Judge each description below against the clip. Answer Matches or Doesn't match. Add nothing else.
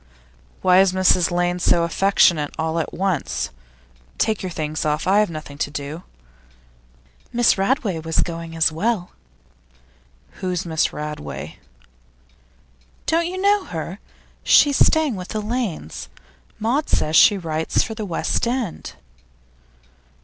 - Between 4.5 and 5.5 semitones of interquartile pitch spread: Matches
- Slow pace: Matches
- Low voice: Doesn't match